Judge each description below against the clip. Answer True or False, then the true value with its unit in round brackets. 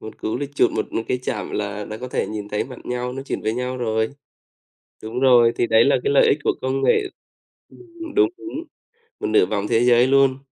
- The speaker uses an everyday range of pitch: True (3.5 semitones)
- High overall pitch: False (125 Hz)